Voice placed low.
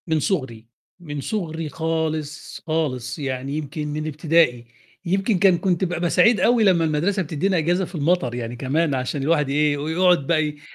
No: medium, 155 Hz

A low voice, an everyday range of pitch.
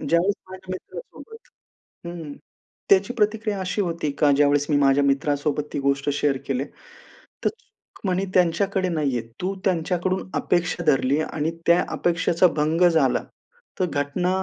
No: medium, 170 Hz; average, 4.4 semitones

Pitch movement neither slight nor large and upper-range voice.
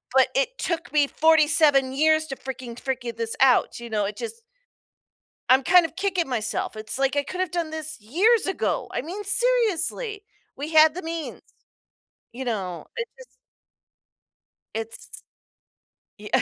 No: wide, 6.2 semitones; very high, 310 Hz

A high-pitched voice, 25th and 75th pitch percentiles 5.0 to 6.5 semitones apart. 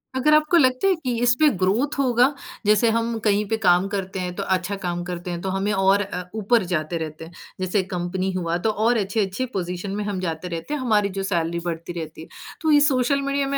Yes: high, 195 Hz; wide, 5.5 semitones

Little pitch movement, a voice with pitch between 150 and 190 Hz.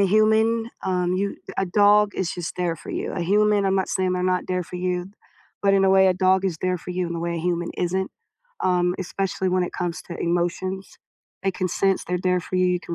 Yes: narrow, 1.4 semitones; medium, 185 Hz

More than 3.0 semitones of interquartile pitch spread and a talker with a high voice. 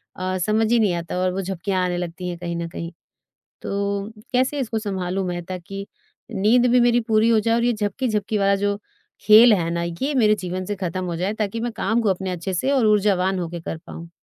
Yes: average, 3.5 semitones; high, 195 Hz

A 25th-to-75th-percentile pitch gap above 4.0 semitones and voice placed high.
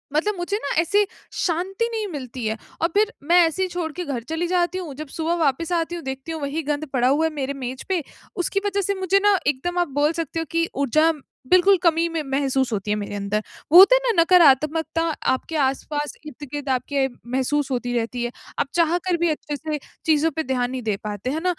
Yes: average, 4.7 semitones; very high, 310 Hz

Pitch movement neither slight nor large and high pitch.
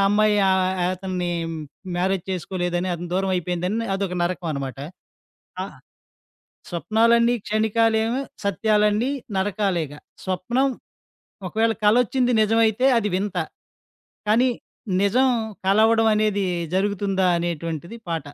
Yes: average, 3.7 semitones; high, 200 Hz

